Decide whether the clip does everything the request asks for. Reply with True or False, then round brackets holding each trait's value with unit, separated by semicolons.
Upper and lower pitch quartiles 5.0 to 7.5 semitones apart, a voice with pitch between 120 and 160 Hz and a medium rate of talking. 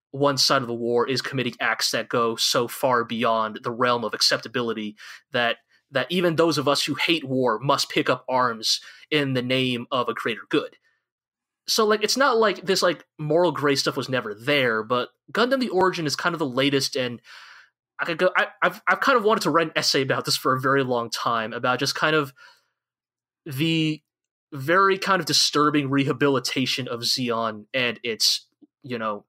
True (5.4 semitones; 140 Hz; 195 wpm)